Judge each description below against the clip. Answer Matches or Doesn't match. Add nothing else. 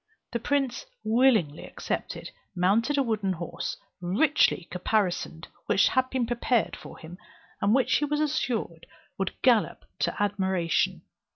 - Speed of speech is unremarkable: Doesn't match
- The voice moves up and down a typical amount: Doesn't match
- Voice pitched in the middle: Doesn't match